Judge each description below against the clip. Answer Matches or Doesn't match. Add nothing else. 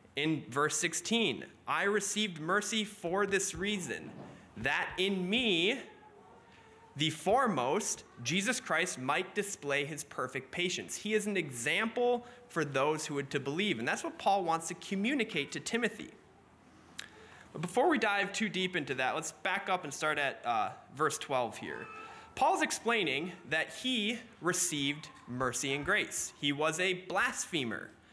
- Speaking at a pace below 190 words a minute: Matches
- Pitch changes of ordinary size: Doesn't match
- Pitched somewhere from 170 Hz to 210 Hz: Matches